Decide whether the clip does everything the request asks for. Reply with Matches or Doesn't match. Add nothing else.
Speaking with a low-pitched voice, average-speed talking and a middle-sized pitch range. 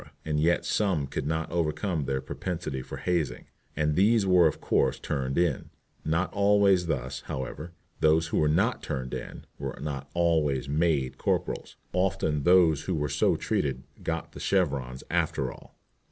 Matches